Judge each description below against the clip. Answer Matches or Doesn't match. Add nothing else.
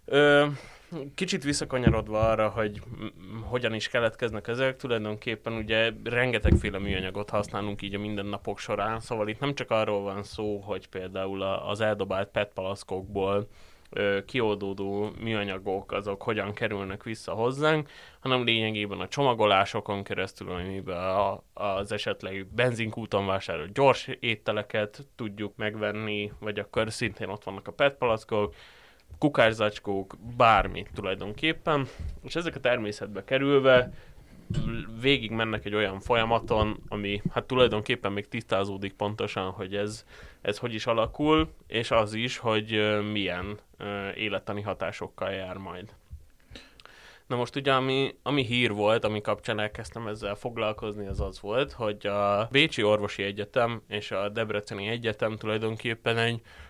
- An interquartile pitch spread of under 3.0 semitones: Matches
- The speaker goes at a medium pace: Matches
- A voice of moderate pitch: Doesn't match